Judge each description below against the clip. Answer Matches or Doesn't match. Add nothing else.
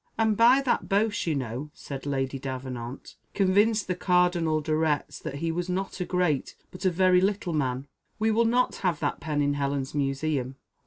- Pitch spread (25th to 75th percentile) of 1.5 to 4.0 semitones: Doesn't match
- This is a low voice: Doesn't match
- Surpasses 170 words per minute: Matches